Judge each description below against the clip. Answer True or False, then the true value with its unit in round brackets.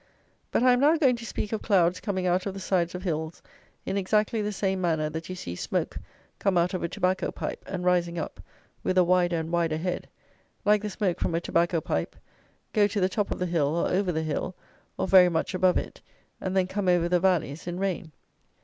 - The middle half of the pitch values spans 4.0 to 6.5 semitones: False (2.4 semitones)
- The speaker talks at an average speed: False (230 wpm)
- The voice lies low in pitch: False (180 Hz)